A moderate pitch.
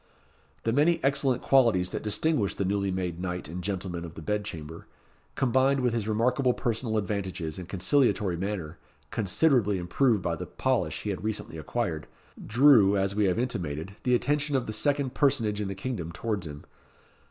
No: low, 105 Hz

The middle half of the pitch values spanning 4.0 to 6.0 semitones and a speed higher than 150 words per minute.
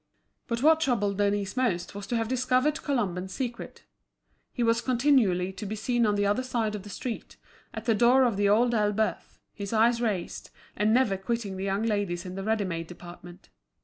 No: average, 3.6 semitones; average, 195 wpm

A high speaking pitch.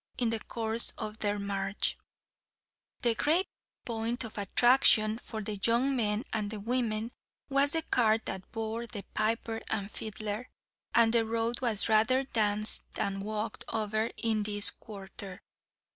Yes: high, 220 Hz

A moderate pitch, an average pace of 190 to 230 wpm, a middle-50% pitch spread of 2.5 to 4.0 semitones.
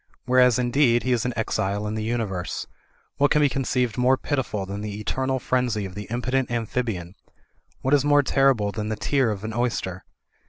No: low, 120 Hz; average, 200 wpm; average, 3.6 semitones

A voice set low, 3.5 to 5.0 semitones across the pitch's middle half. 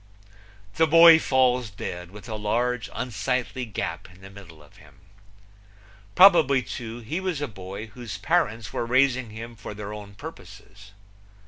Yes: low, 115 Hz; average, 4.2 semitones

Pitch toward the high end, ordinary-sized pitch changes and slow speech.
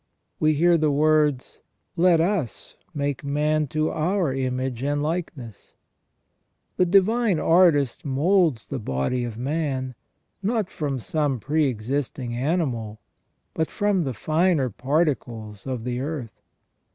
No: medium, 145 Hz; average, 4.4 semitones; slow, 130 wpm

